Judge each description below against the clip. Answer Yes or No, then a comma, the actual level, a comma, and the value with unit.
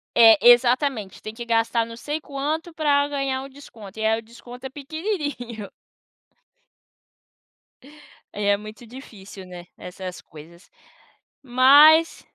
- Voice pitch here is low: No, high, 240 Hz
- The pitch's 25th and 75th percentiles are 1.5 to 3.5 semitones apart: No, average, 4.8 semitones